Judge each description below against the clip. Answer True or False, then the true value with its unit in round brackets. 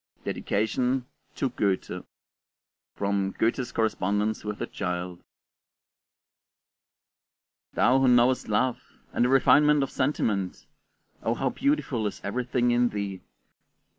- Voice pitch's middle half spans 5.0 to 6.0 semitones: False (4.2 semitones)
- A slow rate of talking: True (105 wpm)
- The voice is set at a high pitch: False (120 Hz)